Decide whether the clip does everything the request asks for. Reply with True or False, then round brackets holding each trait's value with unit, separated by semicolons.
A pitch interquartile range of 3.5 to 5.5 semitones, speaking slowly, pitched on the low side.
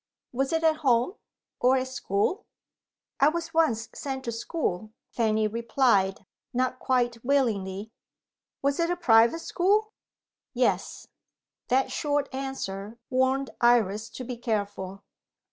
False (4.1 semitones; 125 wpm; 250 Hz)